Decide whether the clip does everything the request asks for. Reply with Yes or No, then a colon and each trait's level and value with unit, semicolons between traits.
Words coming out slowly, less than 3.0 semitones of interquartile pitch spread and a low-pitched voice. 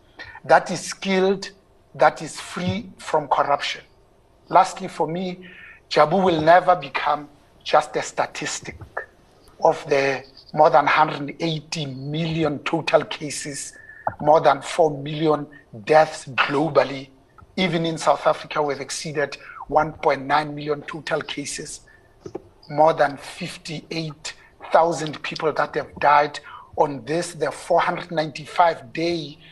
No: slow, 110 wpm; narrow, 2.6 semitones; medium, 155 Hz